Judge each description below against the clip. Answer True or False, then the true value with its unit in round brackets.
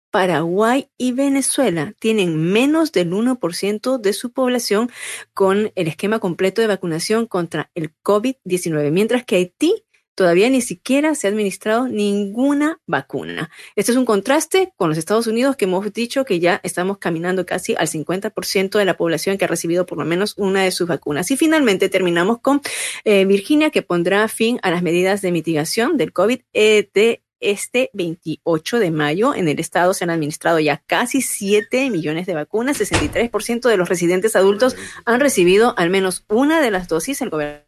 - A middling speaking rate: True (175 wpm)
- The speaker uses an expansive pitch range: True (5.8 semitones)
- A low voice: False (200 Hz)